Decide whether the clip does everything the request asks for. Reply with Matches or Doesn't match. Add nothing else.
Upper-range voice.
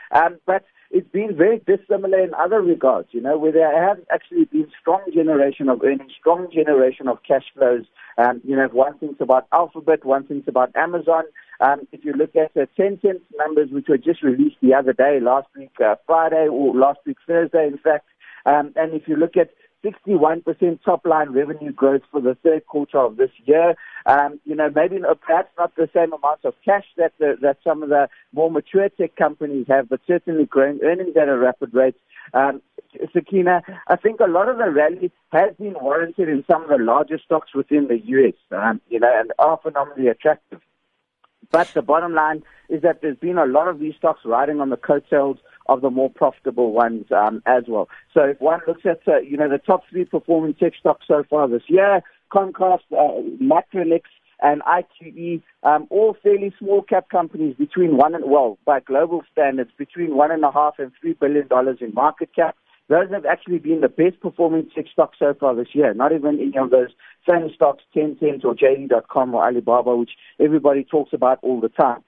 Doesn't match